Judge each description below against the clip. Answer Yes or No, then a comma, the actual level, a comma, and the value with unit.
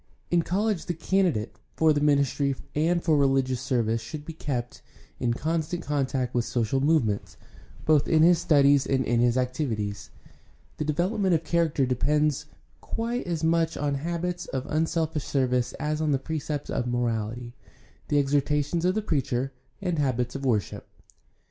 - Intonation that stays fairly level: No, average, 4.2 semitones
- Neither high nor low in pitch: Yes, medium, 145 Hz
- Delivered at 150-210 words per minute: Yes, average, 160 wpm